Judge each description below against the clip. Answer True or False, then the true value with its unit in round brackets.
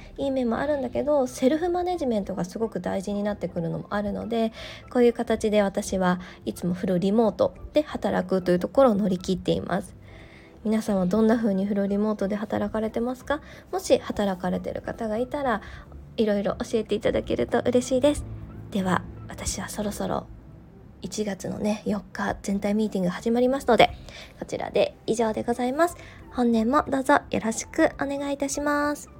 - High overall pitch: True (220 Hz)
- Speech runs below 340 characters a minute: False (375 characters per minute)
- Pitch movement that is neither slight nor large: True (4.3 semitones)